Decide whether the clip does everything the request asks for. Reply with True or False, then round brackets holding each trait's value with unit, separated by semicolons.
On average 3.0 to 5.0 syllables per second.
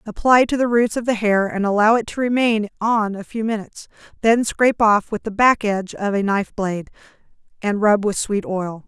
False (5.4 syllables/s)